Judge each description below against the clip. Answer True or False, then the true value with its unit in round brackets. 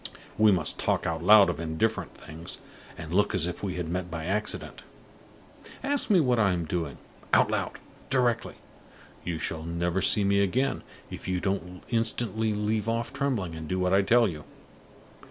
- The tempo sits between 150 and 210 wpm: True (175 wpm)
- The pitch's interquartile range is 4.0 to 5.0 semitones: True (4.6 semitones)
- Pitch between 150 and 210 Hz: False (95 Hz)